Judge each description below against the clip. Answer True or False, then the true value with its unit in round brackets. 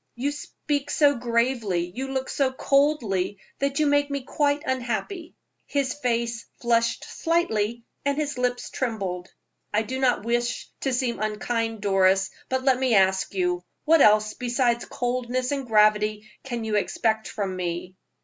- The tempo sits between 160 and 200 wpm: False (150 wpm)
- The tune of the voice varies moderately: True (4.0 semitones)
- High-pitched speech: True (240 Hz)